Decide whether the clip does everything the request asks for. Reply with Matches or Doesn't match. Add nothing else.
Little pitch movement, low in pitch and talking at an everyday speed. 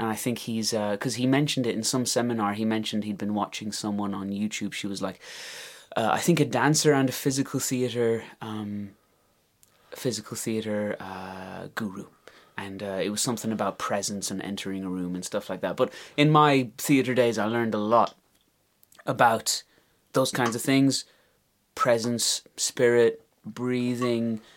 Doesn't match